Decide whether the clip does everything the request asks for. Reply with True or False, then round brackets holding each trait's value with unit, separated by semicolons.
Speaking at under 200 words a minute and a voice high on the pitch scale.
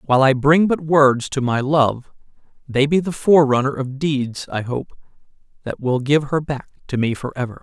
False (190 wpm; 135 Hz)